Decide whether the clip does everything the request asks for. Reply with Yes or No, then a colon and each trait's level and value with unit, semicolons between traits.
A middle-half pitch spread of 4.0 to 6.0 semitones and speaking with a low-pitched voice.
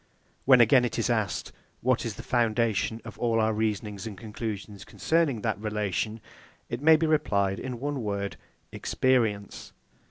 No: average, 2.9 semitones; low, 110 Hz